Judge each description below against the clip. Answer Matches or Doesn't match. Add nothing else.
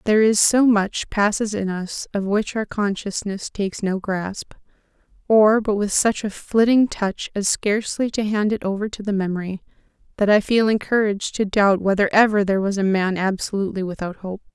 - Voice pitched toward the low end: Doesn't match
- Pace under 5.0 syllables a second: Doesn't match